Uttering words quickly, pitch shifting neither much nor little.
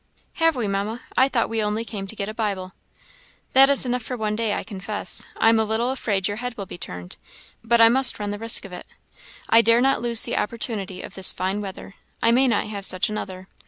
Yes: fast, 235 wpm; average, 3.0 semitones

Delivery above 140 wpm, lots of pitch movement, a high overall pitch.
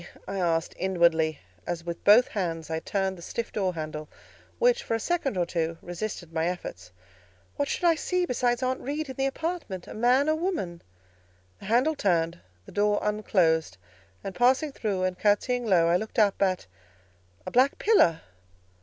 Yes: average, 170 wpm; wide, 7.1 semitones; high, 195 Hz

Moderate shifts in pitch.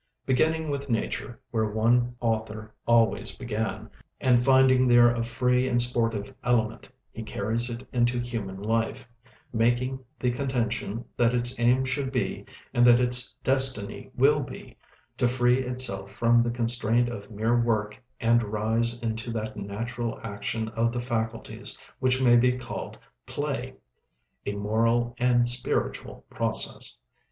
No: narrow, 1.7 semitones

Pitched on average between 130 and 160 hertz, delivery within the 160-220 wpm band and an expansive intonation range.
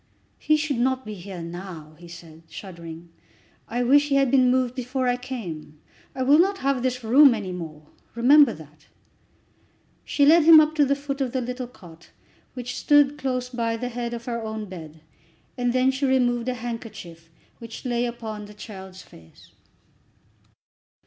No: high, 240 Hz; average, 175 wpm; wide, 5.7 semitones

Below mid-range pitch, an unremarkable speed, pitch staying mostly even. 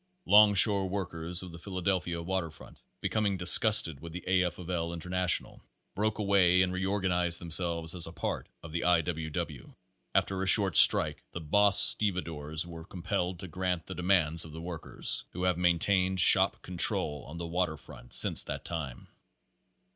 Yes: very low, 90 Hz; average, 170 wpm; narrow, 2.2 semitones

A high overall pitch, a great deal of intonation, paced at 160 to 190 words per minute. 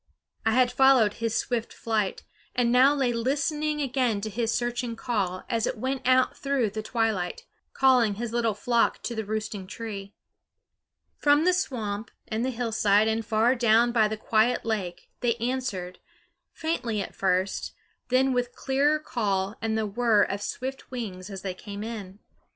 No: high, 230 Hz; average, 3.3 semitones; average, 165 wpm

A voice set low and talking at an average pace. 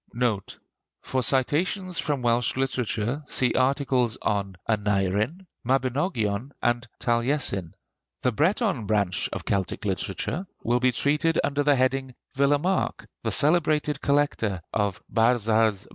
No: low, 125 Hz; slow, 120 wpm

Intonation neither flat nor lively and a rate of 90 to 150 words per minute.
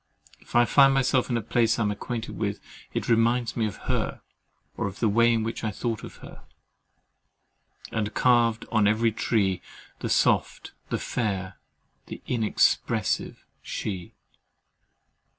No: narrow, 2.1 semitones; average, 145 wpm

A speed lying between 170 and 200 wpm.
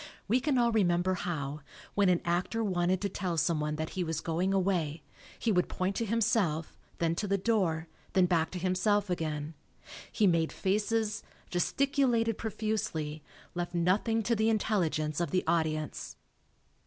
No: average, 160 wpm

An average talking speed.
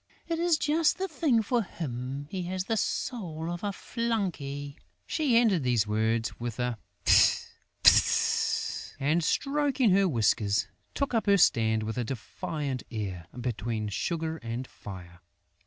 Yes: average, 145 wpm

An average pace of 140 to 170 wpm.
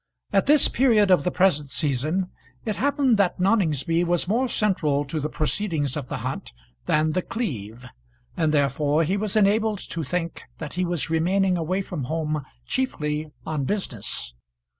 Yes: average, 160 wpm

